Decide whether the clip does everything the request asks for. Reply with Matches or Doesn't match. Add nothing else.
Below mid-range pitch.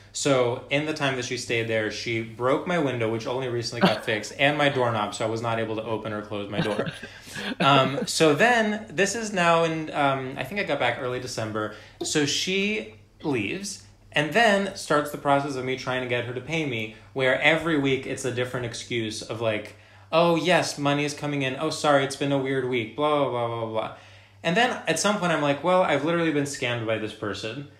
Matches